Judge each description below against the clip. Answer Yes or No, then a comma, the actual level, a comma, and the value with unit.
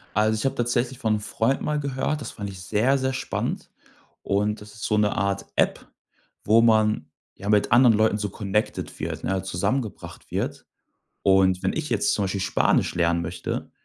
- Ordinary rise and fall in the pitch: Yes, average, 3.5 semitones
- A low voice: Yes, low, 105 Hz